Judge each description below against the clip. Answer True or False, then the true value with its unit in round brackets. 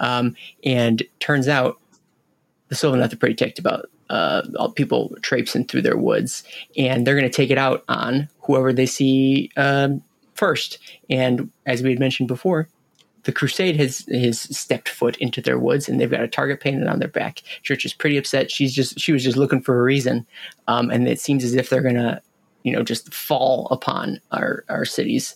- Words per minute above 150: True (200 wpm)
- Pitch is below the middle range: True (130 Hz)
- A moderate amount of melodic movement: False (1.6 semitones)